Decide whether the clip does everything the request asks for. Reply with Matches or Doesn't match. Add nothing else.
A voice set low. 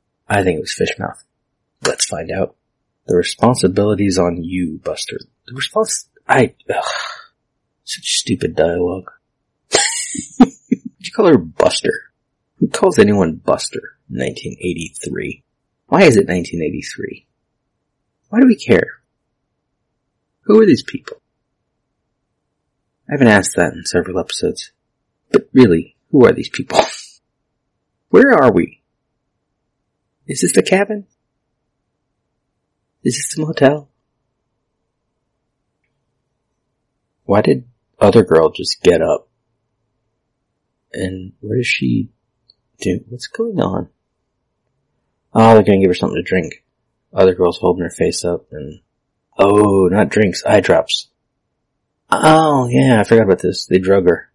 Matches